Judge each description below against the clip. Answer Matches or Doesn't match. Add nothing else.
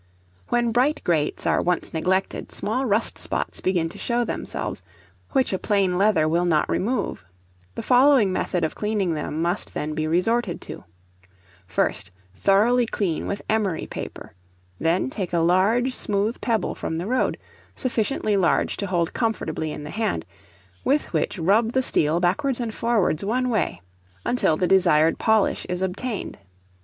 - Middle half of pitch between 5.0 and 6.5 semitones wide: Matches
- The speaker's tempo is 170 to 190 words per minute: Doesn't match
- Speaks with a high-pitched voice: Matches